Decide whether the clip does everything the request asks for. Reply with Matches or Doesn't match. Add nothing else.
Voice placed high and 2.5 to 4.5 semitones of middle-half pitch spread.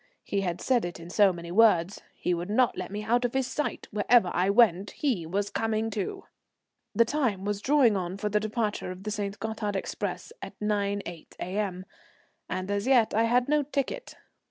Matches